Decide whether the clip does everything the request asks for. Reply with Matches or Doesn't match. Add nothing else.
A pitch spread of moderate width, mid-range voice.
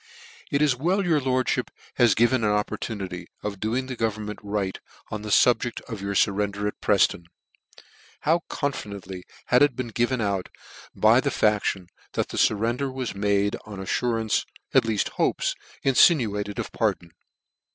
Doesn't match